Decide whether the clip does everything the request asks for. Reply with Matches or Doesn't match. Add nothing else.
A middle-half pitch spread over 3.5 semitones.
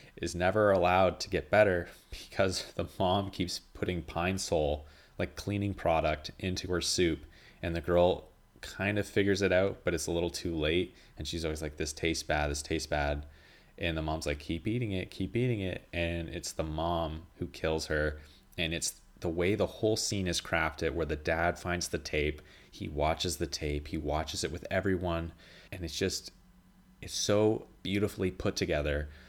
Doesn't match